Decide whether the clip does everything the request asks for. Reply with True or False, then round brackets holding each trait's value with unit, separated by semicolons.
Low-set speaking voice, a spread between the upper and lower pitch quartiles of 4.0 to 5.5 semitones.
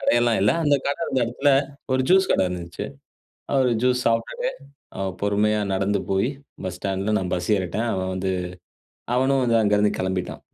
True (105 Hz; 4.9 semitones)